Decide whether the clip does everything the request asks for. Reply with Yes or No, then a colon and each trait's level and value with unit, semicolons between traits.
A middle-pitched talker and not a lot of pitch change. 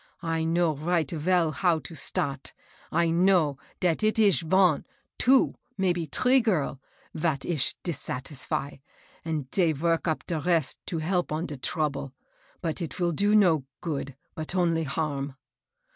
No: medium, 165 Hz; average, 3.0 semitones